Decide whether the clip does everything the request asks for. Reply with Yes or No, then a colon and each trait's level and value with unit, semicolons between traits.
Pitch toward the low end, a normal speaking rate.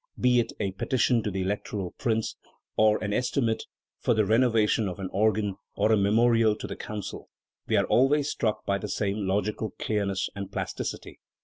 Yes: low, 105 Hz; average, 180 wpm